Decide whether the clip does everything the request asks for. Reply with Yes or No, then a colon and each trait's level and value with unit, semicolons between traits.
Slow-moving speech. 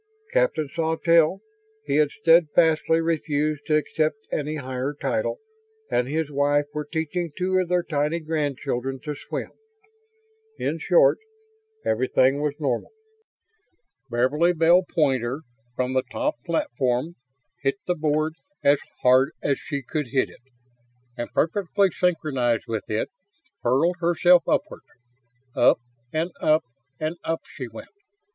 Yes: slow, 125 wpm